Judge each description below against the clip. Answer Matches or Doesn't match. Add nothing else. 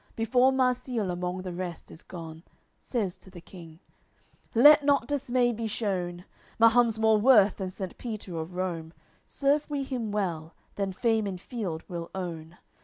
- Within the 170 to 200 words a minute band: Doesn't match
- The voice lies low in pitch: Doesn't match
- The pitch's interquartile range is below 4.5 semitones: Doesn't match